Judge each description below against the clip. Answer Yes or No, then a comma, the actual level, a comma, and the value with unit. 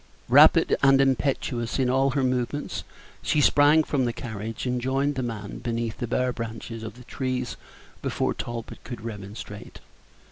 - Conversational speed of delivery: Yes, average, 155 wpm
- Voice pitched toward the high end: No, low, 125 Hz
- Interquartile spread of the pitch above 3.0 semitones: No, average, 2.7 semitones